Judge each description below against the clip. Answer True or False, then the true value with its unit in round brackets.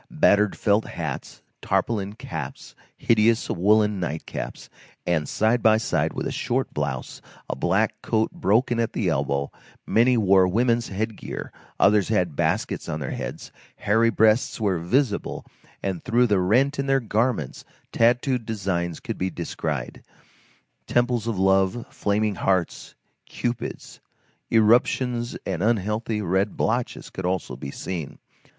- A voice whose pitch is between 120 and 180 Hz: False (105 Hz)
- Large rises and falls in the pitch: False (3.9 semitones)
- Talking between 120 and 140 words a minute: True (135 wpm)